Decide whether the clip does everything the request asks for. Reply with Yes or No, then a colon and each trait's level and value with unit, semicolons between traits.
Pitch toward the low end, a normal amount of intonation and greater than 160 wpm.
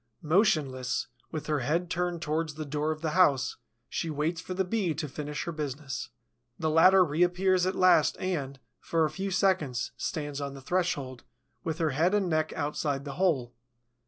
No: medium, 155 Hz; average, 3.7 semitones; average, 180 wpm